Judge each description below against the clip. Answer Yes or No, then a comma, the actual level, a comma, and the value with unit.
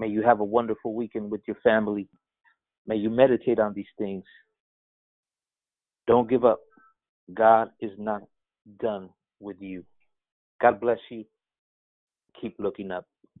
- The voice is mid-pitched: No, low, 110 Hz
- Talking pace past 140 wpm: No, slow, 135 wpm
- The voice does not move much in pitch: No, average, 3.3 semitones